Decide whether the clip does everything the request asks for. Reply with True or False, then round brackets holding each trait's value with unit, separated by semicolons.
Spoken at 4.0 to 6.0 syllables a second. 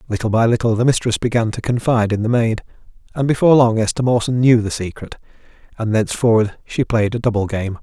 False (6.4 syllables/s)